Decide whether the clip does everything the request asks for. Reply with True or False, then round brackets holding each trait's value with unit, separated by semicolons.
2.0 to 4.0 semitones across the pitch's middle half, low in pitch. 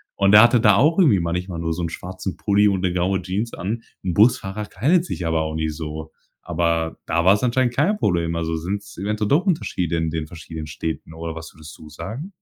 False (4.5 semitones; 90 Hz)